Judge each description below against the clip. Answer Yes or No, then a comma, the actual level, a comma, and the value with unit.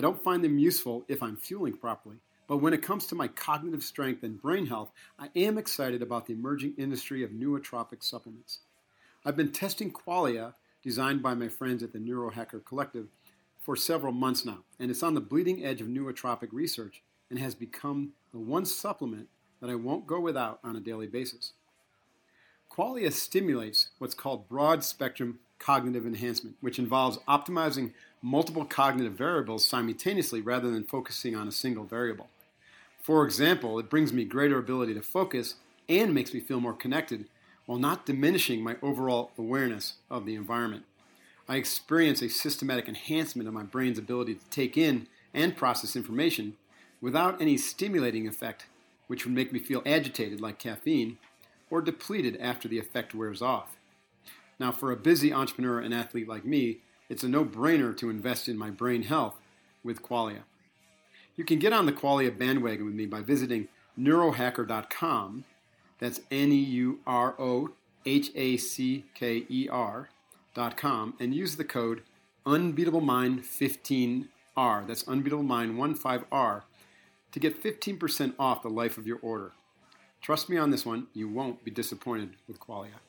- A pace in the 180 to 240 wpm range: No, average, 160 wpm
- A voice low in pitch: Yes, low, 125 Hz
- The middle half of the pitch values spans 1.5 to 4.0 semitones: Yes, average, 3.6 semitones